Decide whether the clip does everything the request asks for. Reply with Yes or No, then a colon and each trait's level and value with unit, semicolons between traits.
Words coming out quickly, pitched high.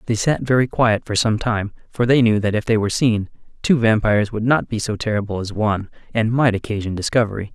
No: fast, 225 wpm; low, 110 Hz